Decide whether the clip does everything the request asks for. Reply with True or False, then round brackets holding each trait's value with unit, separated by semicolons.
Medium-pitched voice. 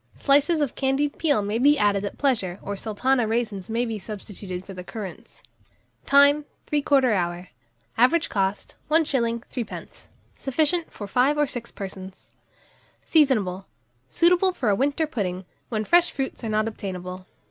False (230 Hz)